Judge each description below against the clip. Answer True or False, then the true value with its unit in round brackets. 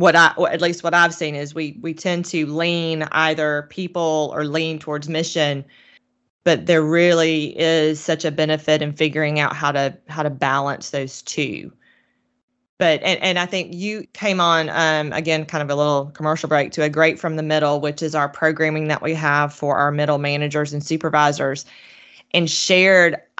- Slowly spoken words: False (190 wpm)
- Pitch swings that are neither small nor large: False (2.0 semitones)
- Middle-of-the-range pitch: True (155 Hz)